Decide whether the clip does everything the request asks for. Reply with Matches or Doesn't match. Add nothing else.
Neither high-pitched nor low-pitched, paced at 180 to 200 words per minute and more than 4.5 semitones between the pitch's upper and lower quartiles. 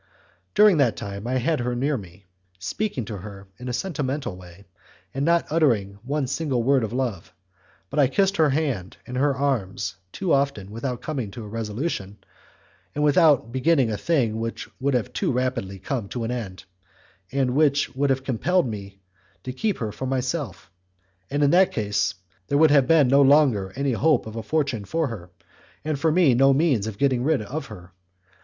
Doesn't match